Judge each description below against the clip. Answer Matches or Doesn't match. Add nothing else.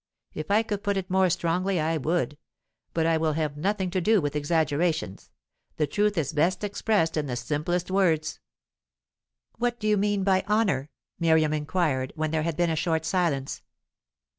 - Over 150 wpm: Matches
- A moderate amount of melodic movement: Matches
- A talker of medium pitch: Matches